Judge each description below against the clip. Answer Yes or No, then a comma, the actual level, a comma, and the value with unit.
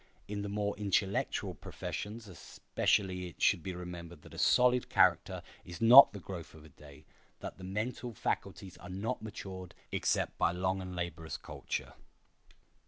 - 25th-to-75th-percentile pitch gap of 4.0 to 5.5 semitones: No, average, 3.0 semitones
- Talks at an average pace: Yes, average, 160 wpm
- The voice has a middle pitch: No, very low, 95 Hz